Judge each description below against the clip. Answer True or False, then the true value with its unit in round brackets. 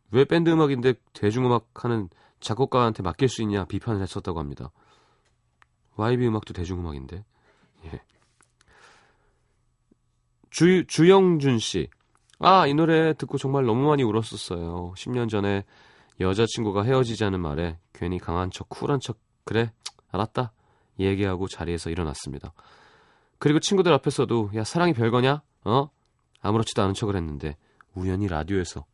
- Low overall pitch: True (110 Hz)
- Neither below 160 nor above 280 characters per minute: False (305 characters per minute)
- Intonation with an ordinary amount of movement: False (6.0 semitones)